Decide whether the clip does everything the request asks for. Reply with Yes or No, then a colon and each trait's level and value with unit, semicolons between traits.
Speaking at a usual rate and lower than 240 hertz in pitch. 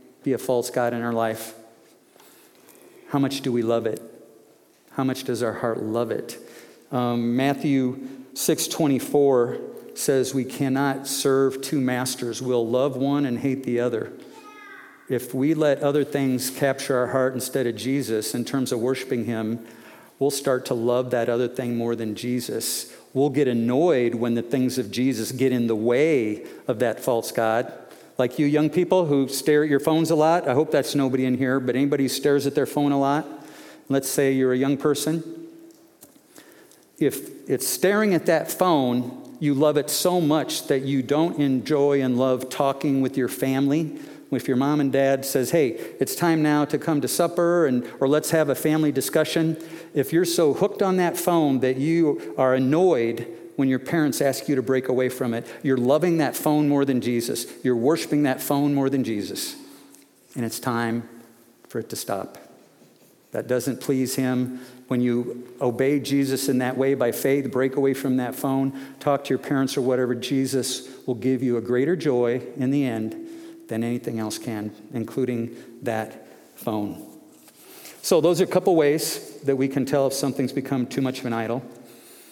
Yes: average, 185 wpm; low, 135 Hz